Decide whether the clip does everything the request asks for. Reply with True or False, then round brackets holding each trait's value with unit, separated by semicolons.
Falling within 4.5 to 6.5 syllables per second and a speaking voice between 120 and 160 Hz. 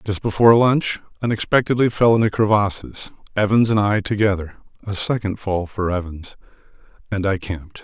False (5.4 syllables/s; 105 Hz)